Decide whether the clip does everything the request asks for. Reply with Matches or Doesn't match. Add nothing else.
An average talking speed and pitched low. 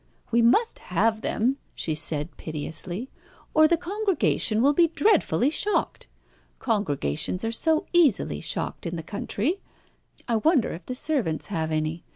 Doesn't match